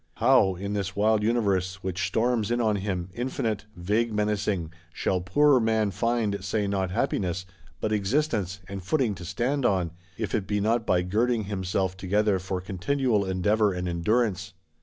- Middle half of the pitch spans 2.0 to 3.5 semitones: Yes, average, 3.1 semitones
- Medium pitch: No, low, 100 Hz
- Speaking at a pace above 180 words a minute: No, average, 160 wpm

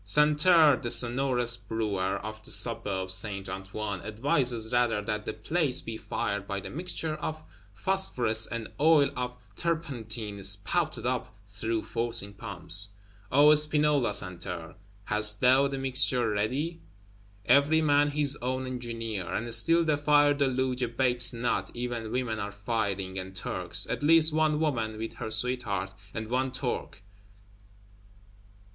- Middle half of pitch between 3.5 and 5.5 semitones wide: Yes, average, 5.2 semitones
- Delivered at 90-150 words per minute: Yes, average, 140 wpm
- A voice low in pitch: Yes, low, 120 Hz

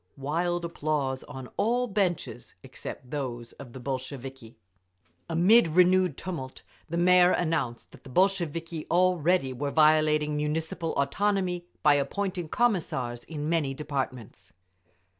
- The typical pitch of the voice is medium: Yes, medium, 155 Hz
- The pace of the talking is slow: Yes, slow, 120 wpm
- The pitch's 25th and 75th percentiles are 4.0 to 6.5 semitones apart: Yes, average, 4.7 semitones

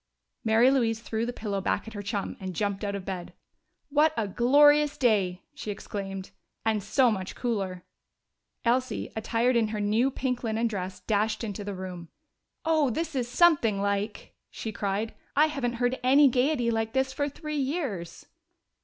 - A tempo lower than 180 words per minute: Yes, average, 170 wpm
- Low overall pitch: No, high, 225 Hz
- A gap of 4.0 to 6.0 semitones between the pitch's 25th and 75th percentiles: Yes, average, 4.5 semitones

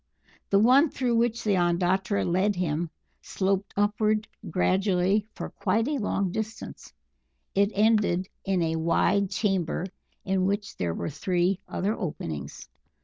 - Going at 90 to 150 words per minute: Yes, slow, 135 wpm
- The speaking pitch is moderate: No, high, 195 Hz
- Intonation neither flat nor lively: Yes, average, 3.0 semitones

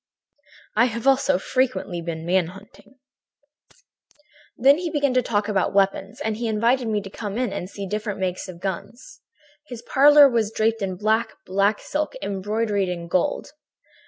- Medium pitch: No, high, 215 Hz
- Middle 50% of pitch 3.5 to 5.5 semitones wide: Yes, average, 4.1 semitones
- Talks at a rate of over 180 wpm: No, average, 160 wpm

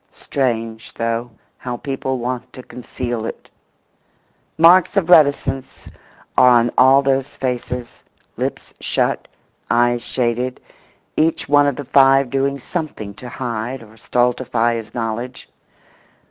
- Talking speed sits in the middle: No, slow, 120 wpm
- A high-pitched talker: No, low, 125 Hz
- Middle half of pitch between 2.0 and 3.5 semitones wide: Yes, narrow, 2.4 semitones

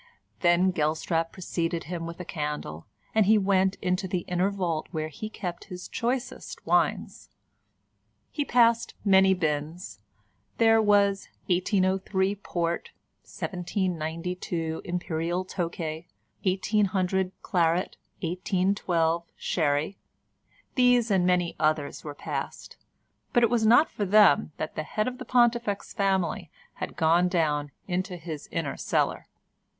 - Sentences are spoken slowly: Yes, slow, 125 wpm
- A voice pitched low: No, medium, 180 Hz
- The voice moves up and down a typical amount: Yes, average, 3.2 semitones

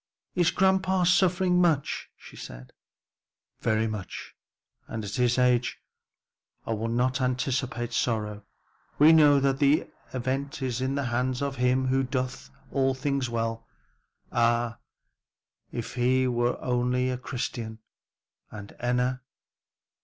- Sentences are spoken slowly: Yes, slow, 130 wpm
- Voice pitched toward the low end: Yes, low, 125 Hz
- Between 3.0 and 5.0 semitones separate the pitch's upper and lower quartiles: No, narrow, 2.6 semitones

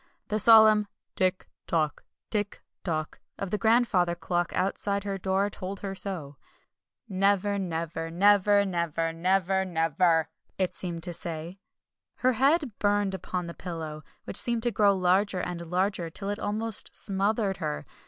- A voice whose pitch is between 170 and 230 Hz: Yes, high, 190 Hz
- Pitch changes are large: No, average, 3.1 semitones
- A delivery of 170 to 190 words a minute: No, average, 145 wpm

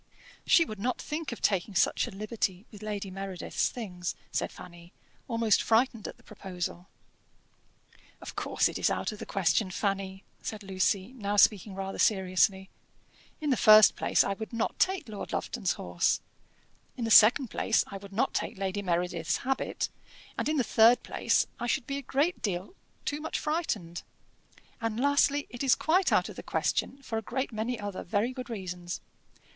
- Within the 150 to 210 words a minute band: Yes, average, 175 wpm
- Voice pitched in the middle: No, high, 215 Hz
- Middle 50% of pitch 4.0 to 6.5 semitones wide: Yes, average, 4.4 semitones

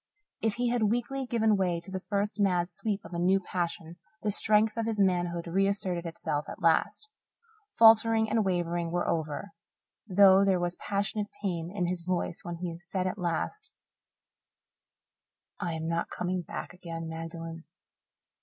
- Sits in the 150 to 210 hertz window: Yes, medium, 185 Hz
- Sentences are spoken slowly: No, average, 160 wpm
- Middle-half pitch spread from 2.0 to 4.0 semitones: Yes, average, 3.4 semitones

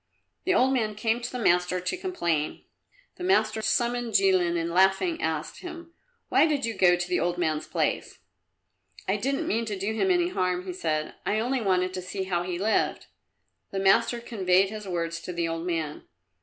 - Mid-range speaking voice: No, high, 195 Hz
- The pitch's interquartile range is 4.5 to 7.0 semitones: Yes, average, 5.1 semitones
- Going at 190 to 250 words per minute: Yes, average, 195 wpm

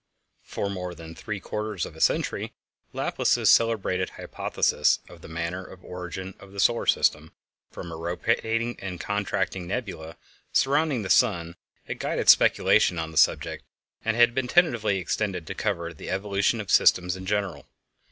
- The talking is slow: No, average, 160 wpm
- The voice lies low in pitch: Yes, very low, 95 Hz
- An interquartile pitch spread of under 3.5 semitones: No, average, 3.8 semitones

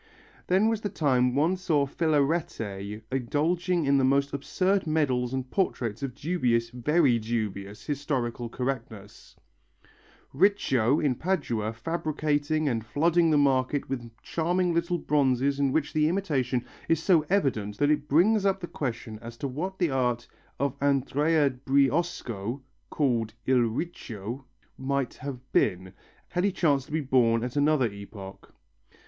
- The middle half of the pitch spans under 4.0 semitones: No, average, 4.9 semitones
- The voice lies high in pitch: No, medium, 140 Hz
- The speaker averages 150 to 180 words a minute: No, average, 140 wpm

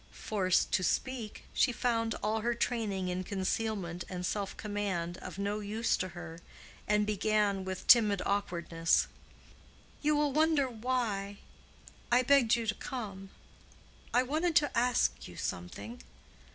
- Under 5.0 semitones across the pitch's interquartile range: Yes, average, 4.2 semitones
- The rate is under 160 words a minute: Yes, average, 140 wpm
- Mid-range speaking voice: No, high, 210 Hz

